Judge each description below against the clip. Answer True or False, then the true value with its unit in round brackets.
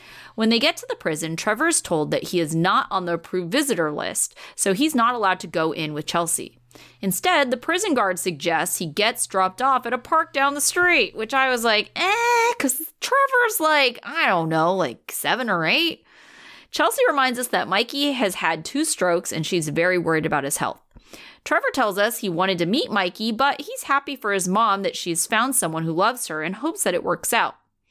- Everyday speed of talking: False (215 wpm)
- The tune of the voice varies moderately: False (8.3 semitones)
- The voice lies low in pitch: False (210 Hz)